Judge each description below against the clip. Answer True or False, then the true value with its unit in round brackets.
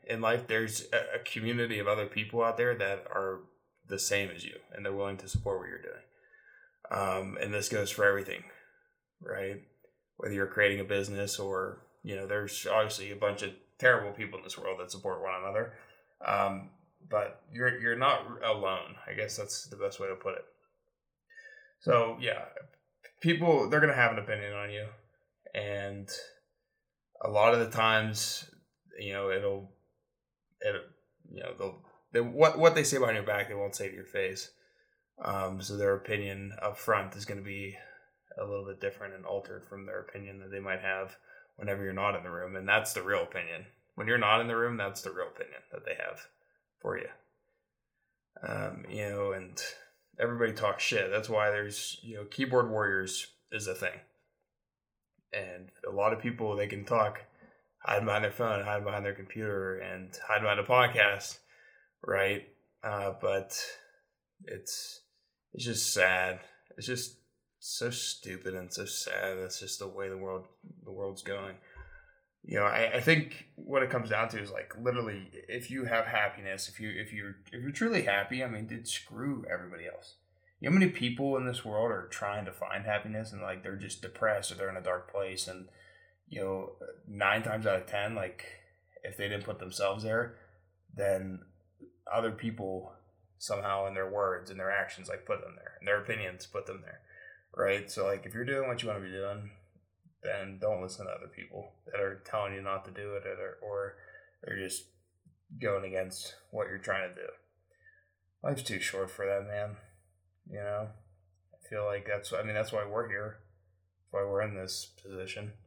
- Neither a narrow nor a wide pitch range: True (3.9 semitones)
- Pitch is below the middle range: True (105 Hz)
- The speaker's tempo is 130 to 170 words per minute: False (190 wpm)